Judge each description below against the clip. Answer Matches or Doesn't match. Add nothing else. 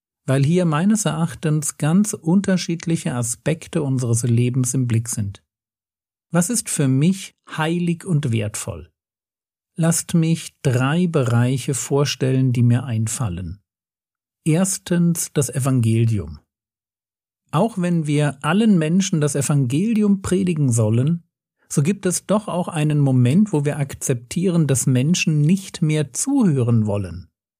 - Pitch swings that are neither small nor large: Doesn't match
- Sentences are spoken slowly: Matches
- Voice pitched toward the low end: Doesn't match